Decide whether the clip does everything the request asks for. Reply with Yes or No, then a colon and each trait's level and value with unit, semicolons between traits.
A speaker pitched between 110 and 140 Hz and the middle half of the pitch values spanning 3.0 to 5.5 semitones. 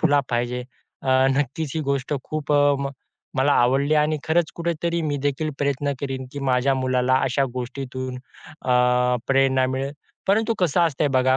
No: low, 135 Hz; narrow, 2.5 semitones